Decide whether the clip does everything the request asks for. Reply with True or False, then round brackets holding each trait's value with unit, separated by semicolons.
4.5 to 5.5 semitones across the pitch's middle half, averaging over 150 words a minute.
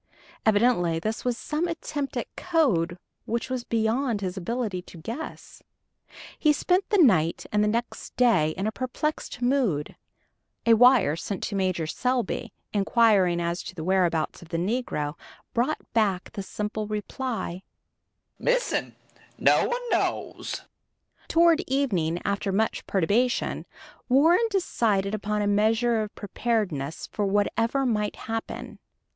False (5.0 semitones; 135 wpm)